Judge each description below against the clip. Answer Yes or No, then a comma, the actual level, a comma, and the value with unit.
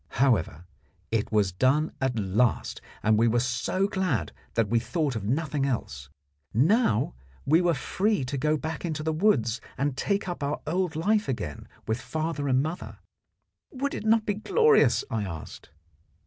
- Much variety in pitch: Yes, wide, 7.4 semitones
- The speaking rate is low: No, average, 165 wpm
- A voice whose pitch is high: No, medium, 140 Hz